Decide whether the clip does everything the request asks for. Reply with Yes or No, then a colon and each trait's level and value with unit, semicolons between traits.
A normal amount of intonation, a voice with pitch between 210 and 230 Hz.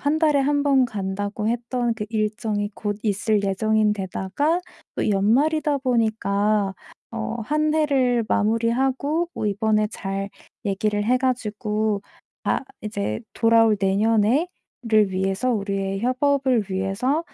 Yes: average, 3.9 semitones; high, 220 Hz